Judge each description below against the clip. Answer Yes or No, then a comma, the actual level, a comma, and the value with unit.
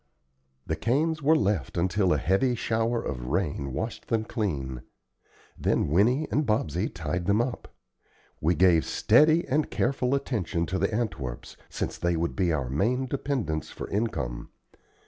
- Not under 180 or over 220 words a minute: No, average, 150 wpm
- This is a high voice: No, low, 100 Hz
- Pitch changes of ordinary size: No, wide, 7.2 semitones